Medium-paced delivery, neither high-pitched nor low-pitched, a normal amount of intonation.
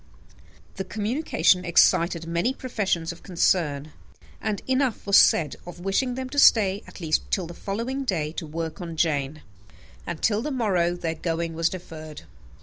Yes: average, 160 wpm; medium, 175 Hz; average, 4.6 semitones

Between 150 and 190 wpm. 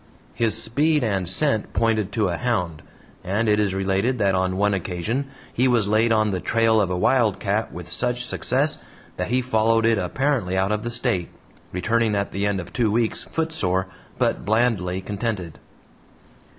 Yes: average, 175 wpm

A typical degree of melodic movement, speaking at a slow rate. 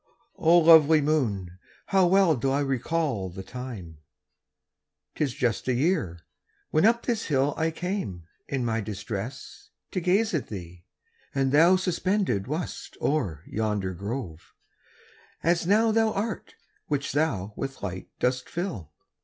No: wide, 8.7 semitones; slow, 130 wpm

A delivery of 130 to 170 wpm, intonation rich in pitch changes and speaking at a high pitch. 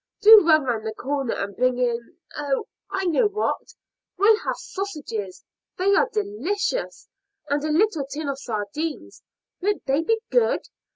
Yes: average, 155 wpm; wide, 7.8 semitones; very high, 310 Hz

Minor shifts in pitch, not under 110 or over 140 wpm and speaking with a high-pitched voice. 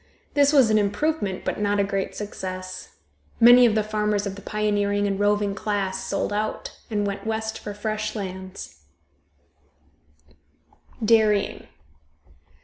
Yes: narrow, 1.4 semitones; slow, 135 wpm; high, 205 Hz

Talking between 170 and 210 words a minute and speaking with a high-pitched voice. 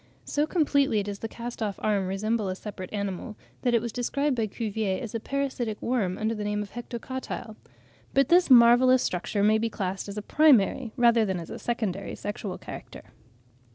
Yes: average, 190 wpm; high, 220 Hz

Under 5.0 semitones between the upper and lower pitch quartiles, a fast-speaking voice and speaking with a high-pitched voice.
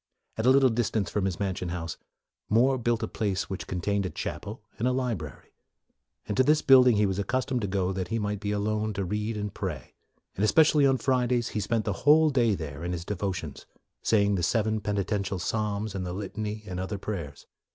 No: average, 3.5 semitones; fast, 215 wpm; low, 105 Hz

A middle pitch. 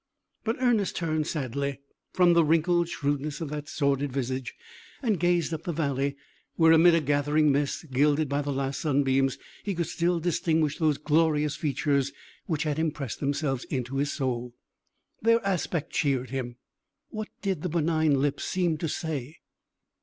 Yes: medium, 150 Hz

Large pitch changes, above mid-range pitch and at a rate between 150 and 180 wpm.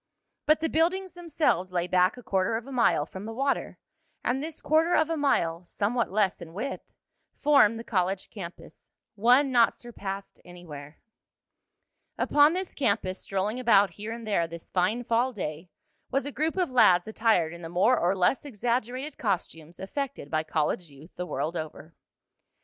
Yes: wide, 6.9 semitones; high, 215 Hz; average, 170 wpm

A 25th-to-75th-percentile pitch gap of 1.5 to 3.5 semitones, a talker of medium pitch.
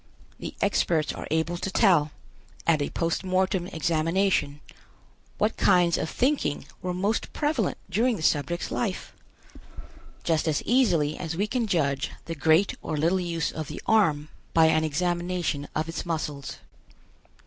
Yes: average, 3.2 semitones; medium, 170 Hz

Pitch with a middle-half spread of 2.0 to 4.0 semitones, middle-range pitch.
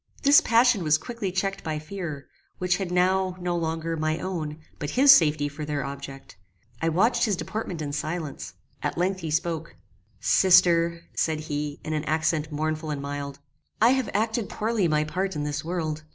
Yes: average, 3.7 semitones; medium, 165 Hz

